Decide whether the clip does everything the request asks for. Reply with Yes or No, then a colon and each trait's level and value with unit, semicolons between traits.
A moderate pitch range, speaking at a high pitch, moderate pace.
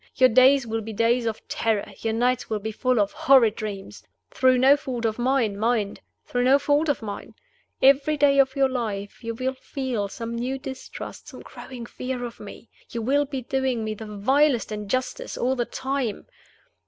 Yes: average, 3.1 semitones; high, 245 Hz; average, 190 wpm